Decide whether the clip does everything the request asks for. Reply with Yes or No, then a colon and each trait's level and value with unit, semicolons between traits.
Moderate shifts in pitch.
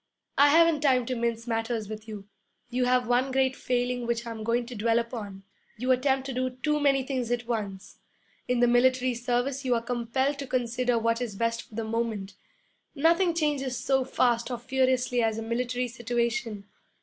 No: narrow, 2.0 semitones